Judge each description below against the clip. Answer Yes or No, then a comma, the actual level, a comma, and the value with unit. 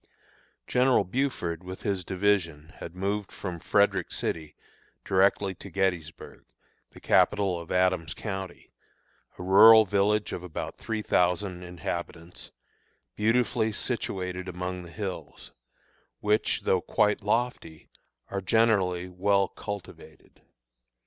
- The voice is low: Yes, very low, 95 Hz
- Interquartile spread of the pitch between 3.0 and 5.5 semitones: No, narrow, 2.6 semitones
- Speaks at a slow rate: Yes, slow, 110 wpm